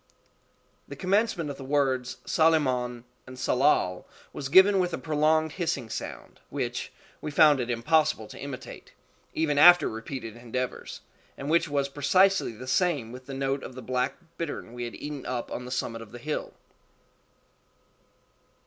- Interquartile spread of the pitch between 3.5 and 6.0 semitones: Yes, average, 3.9 semitones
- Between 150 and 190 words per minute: Yes, average, 155 wpm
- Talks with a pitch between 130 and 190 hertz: Yes, low, 135 Hz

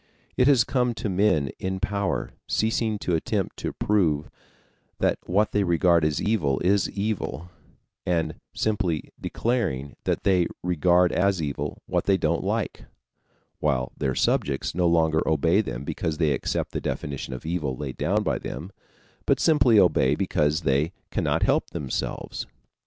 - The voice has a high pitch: No, very low, 85 Hz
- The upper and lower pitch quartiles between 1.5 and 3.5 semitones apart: No, average, 5.1 semitones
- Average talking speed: Yes, average, 150 wpm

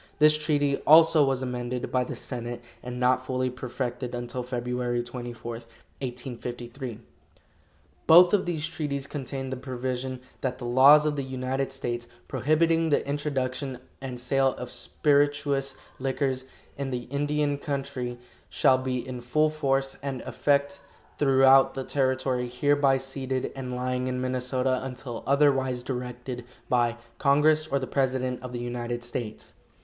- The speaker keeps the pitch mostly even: Yes, narrow, 2.1 semitones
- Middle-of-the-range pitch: No, low, 130 Hz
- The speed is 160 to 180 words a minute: No, average, 140 wpm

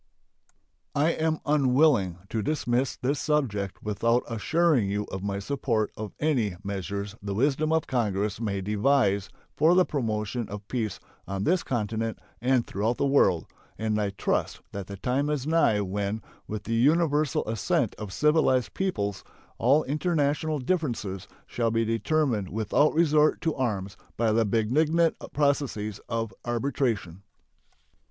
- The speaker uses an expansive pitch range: Yes, wide, 6.2 semitones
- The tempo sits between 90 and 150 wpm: Yes, average, 140 wpm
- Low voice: Yes, low, 115 Hz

